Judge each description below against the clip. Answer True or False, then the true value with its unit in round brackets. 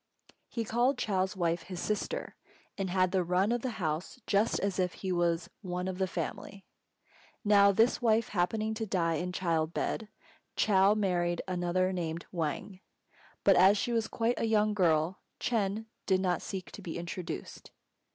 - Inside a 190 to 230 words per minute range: False (170 wpm)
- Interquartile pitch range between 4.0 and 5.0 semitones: False (3.3 semitones)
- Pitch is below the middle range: False (190 Hz)